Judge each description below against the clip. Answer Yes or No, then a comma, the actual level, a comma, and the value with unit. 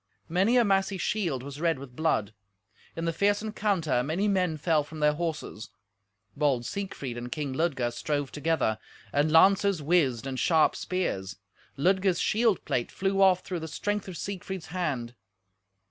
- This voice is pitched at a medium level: Yes, medium, 160 Hz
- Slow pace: No, average, 160 wpm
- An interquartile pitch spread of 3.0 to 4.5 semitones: No, wide, 5.5 semitones